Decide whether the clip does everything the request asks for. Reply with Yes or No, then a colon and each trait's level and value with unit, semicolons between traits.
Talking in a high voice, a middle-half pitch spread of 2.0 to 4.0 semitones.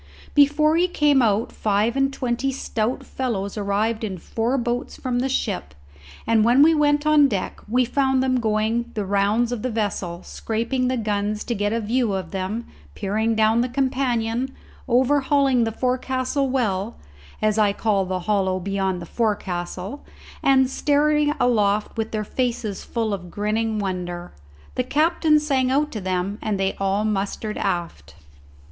No: high, 225 Hz; average, 4.4 semitones